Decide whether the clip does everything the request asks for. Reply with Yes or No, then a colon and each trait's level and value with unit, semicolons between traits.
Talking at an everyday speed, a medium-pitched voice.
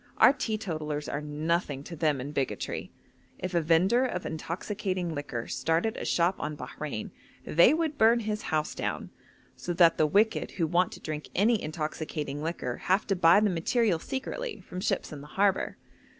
Yes: average, 175 wpm; medium, 170 Hz